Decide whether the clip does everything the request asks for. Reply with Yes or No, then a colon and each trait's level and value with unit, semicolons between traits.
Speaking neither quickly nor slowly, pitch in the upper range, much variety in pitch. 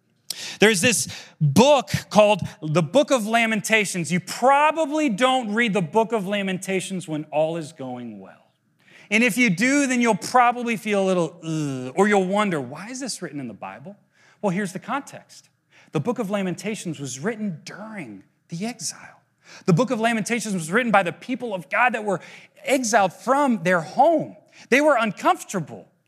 Yes: average, 175 wpm; high, 205 Hz; wide, 5.9 semitones